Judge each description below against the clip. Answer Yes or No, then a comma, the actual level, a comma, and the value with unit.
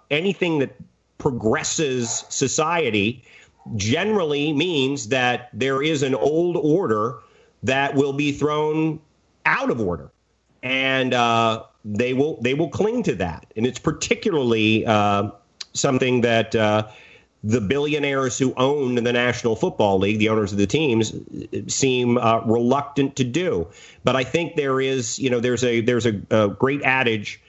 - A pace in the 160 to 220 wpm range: No, average, 145 wpm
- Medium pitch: No, low, 130 Hz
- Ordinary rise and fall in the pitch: Yes, average, 3.9 semitones